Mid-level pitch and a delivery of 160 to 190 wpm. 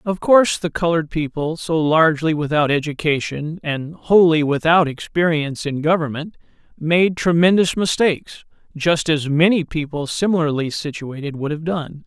No: medium, 160 Hz; slow, 135 wpm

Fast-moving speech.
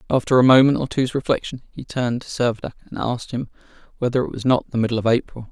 Yes: fast, 230 wpm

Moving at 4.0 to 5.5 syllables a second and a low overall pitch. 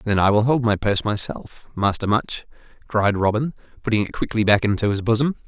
No: 5.8 syllables/s; low, 110 Hz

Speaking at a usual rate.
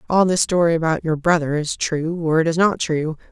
No: fast, 215 wpm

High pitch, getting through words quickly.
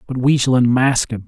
No: low, 125 Hz; fast, 235 wpm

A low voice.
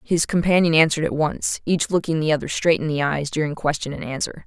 No: medium, 155 Hz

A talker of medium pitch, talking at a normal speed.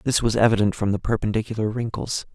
No: low, 110 Hz; average, 180 wpm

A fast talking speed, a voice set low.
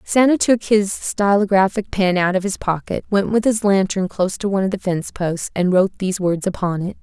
No: fast, 220 wpm; high, 195 Hz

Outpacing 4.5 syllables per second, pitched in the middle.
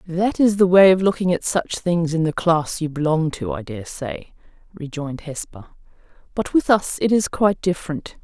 Yes: 5.0 syllables/s; medium, 170 Hz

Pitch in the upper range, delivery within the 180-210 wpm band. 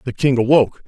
No: low, 125 Hz; fast, 205 wpm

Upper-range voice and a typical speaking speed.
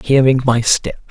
No: low, 130 Hz; average, 165 wpm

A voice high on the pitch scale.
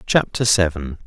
No: very low, 95 Hz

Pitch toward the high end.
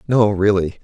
No: low, 100 Hz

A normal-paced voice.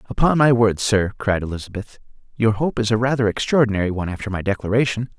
Yes: average, 185 wpm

